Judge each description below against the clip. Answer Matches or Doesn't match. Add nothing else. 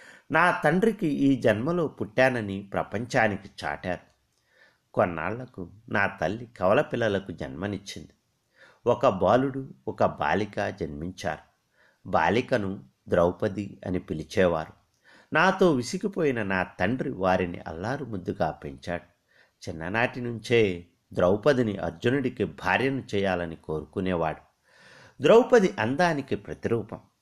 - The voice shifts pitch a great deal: Matches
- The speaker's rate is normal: Matches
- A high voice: Doesn't match